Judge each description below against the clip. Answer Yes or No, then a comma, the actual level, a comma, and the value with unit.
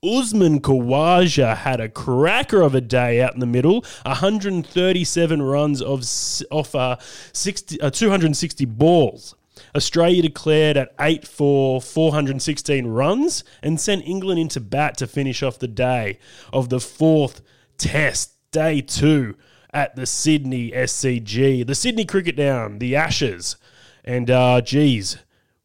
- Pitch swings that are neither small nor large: Yes, average, 4.0 semitones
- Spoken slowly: Yes, slow, 130 wpm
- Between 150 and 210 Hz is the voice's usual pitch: No, medium, 140 Hz